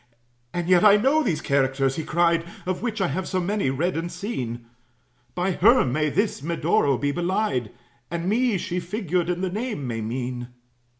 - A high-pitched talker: No, medium, 175 Hz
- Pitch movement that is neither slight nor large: No, wide, 6.1 semitones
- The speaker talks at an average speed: Yes, average, 180 wpm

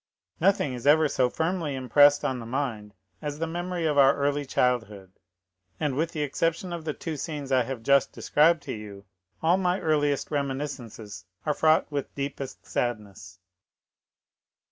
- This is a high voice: No, medium, 140 Hz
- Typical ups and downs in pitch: Yes, average, 4.0 semitones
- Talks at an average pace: Yes, average, 160 wpm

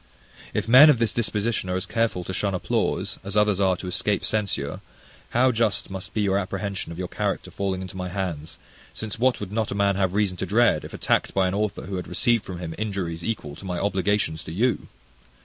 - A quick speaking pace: Yes, fast, 220 wpm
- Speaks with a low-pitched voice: Yes, low, 100 Hz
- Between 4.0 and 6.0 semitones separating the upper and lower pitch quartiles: No, average, 2.7 semitones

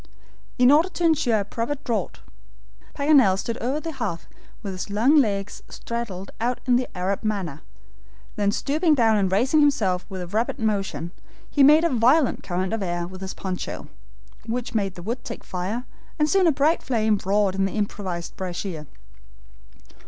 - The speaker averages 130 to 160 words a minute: No, average, 175 wpm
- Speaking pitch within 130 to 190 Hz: No, high, 220 Hz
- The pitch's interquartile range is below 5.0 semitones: No, wide, 5.6 semitones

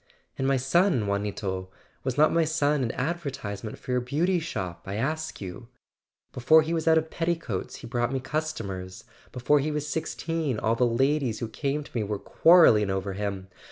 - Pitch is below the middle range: Yes, low, 130 Hz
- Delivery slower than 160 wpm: No, average, 195 wpm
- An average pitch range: No, wide, 6.7 semitones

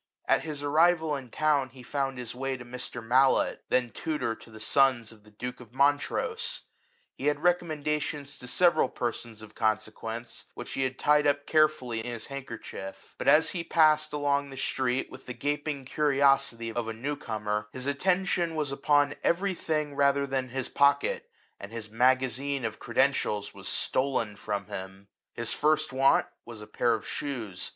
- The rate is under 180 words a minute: No, average, 185 wpm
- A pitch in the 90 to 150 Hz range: Yes, low, 135 Hz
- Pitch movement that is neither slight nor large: Yes, average, 4.0 semitones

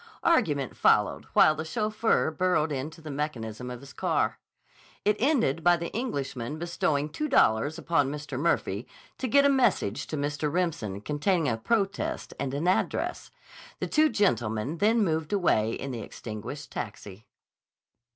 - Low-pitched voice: No, medium, 155 Hz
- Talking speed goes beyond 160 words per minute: No, average, 150 wpm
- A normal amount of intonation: No, wide, 6.4 semitones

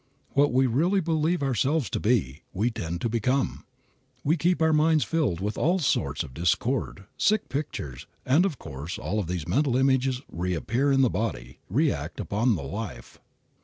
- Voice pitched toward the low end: Yes, low, 125 Hz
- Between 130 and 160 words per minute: No, average, 170 wpm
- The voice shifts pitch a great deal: Yes, wide, 8.3 semitones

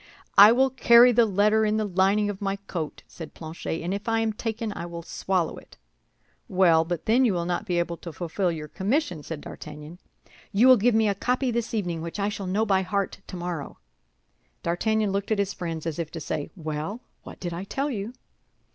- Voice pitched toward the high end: Yes, high, 195 Hz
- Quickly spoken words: Yes, fast, 210 wpm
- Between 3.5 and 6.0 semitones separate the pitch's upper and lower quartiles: Yes, average, 4.3 semitones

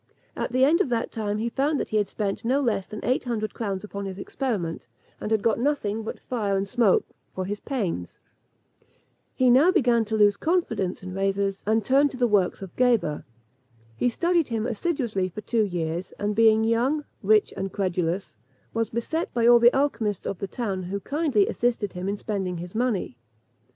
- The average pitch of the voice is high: Yes, high, 215 Hz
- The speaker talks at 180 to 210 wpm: Yes, average, 195 wpm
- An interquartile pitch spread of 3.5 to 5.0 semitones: Yes, average, 3.9 semitones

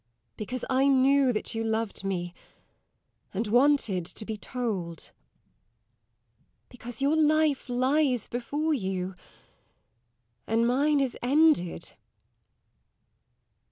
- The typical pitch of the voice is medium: No, high, 245 Hz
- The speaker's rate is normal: No, slow, 95 wpm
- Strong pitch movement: No, average, 4.7 semitones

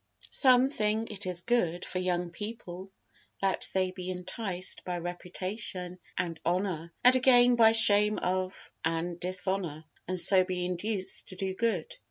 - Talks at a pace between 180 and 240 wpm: No, average, 150 wpm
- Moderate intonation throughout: Yes, average, 3.1 semitones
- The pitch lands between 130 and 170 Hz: No, medium, 185 Hz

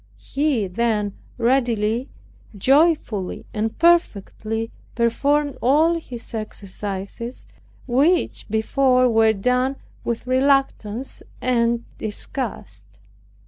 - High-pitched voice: Yes, high, 235 Hz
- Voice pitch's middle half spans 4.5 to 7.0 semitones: No, average, 3.8 semitones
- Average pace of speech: No, slow, 80 wpm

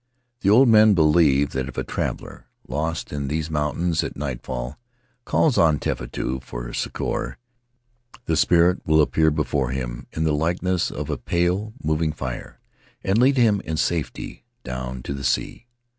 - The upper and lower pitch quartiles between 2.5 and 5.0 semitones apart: Yes, average, 4.6 semitones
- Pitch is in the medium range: No, very low, 80 Hz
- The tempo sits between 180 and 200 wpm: No, average, 160 wpm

